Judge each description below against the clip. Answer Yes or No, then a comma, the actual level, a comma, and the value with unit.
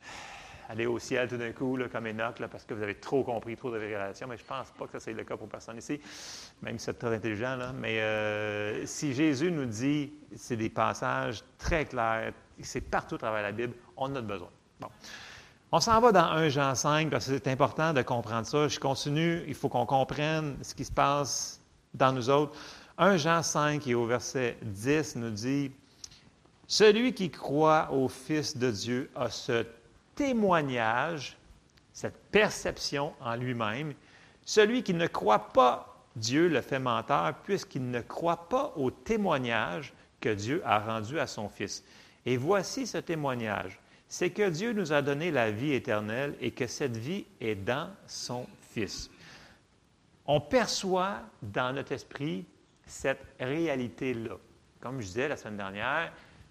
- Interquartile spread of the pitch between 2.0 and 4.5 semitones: No, average, 5.0 semitones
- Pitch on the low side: Yes, low, 130 Hz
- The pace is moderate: Yes, average, 175 wpm